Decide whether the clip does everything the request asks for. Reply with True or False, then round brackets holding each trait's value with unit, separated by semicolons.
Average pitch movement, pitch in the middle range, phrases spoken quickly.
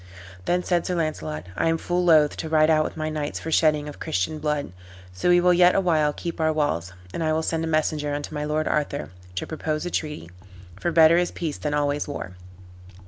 False (1.8 semitones; 155 Hz; 225 wpm)